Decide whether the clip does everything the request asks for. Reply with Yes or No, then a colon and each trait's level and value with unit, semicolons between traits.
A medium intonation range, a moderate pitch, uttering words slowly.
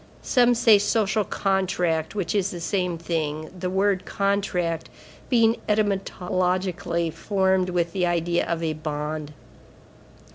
Yes: average, 3.1 semitones; medium, 180 Hz; slow, 120 wpm